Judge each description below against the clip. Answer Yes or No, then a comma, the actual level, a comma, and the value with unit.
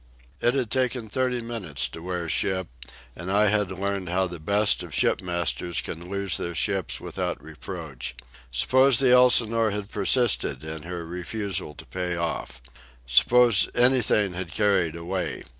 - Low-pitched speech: Yes, very low, 95 Hz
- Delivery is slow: No, average, 145 wpm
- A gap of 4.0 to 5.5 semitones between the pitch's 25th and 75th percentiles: Yes, average, 4.7 semitones